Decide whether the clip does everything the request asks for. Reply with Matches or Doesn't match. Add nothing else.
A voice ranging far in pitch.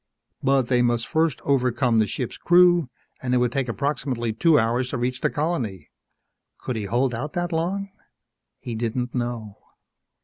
Doesn't match